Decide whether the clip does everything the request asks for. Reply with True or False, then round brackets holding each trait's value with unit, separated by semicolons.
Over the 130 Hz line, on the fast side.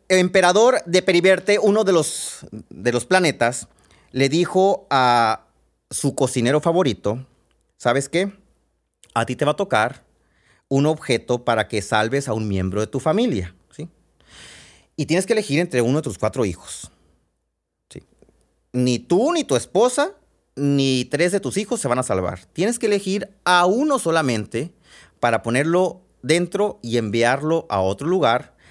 False (140 Hz; 155 wpm)